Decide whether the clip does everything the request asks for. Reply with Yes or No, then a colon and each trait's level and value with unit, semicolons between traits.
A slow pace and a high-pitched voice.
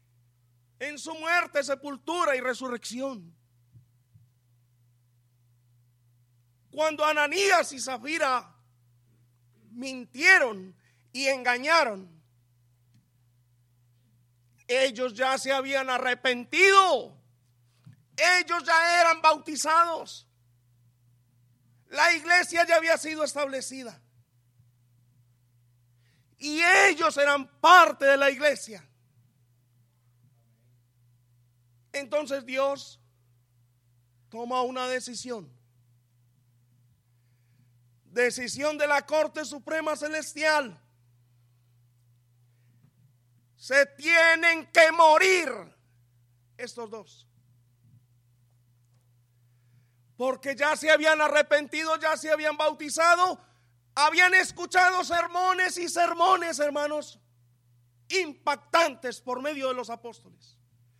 Yes: slow, 70 wpm; high, 195 Hz